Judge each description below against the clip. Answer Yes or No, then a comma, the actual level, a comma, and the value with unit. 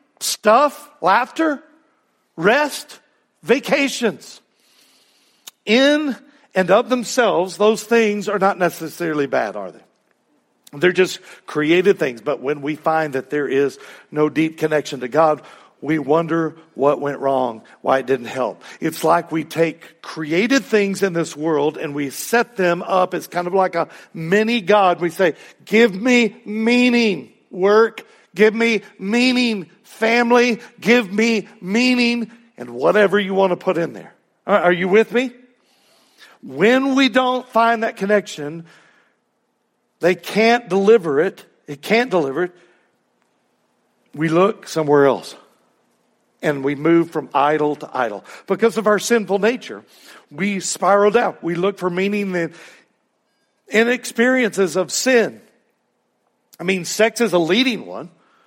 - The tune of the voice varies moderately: No, wide, 6.2 semitones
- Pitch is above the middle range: Yes, high, 195 Hz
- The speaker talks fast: No, average, 140 wpm